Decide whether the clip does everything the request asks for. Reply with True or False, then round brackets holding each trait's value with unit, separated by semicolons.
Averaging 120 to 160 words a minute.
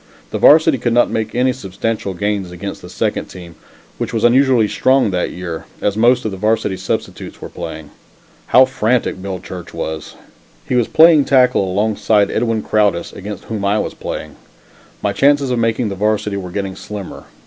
False (180 wpm)